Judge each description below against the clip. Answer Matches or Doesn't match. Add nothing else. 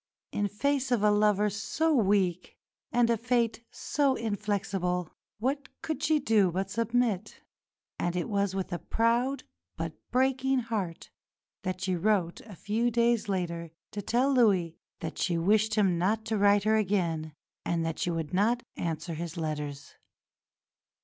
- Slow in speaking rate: Doesn't match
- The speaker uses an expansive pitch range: Doesn't match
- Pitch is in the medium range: Doesn't match